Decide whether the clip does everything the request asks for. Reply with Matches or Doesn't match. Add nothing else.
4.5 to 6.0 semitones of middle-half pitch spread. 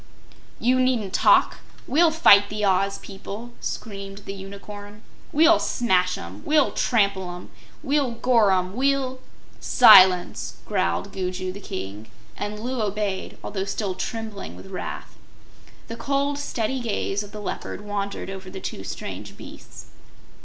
Doesn't match